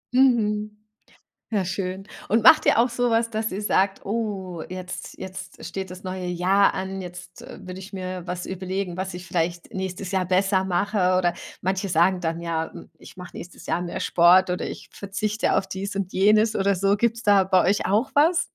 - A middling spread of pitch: No, narrow, 2.3 semitones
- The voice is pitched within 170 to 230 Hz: Yes, high, 190 Hz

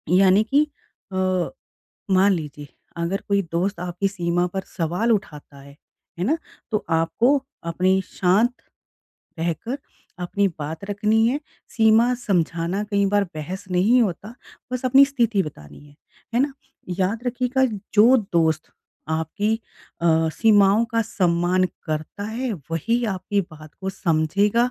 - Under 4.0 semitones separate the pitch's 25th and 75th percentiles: No, average, 4.9 semitones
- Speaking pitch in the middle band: No, high, 195 Hz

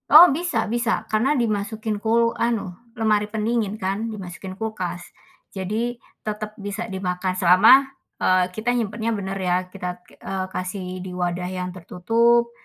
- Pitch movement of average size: Yes, average, 3.7 semitones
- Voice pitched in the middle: No, high, 210 Hz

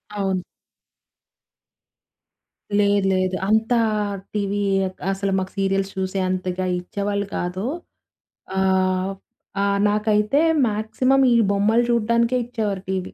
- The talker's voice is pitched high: Yes, high, 200 Hz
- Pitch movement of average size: No, narrow, 2.2 semitones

